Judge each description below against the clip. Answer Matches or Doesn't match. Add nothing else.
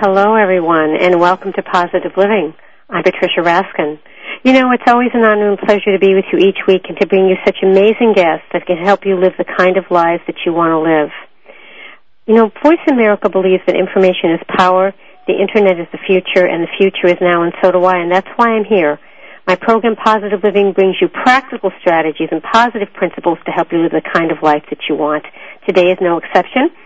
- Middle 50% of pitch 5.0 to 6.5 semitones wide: Doesn't match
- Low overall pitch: Doesn't match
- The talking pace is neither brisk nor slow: Doesn't match